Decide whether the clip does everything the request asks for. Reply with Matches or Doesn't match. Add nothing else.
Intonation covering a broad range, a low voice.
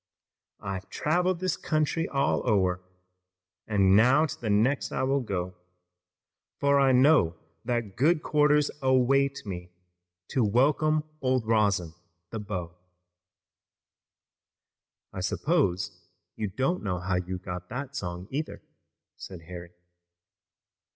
Matches